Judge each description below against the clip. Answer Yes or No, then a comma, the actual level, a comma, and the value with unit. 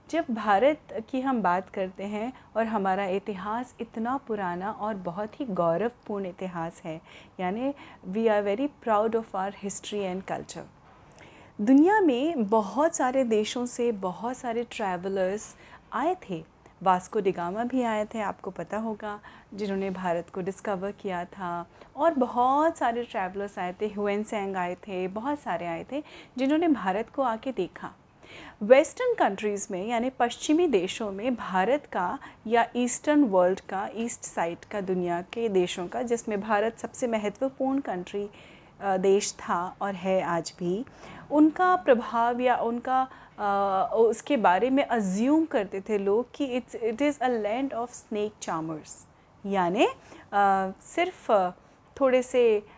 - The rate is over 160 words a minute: No, average, 145 wpm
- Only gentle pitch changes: No, average, 4.7 semitones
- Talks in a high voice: Yes, high, 215 Hz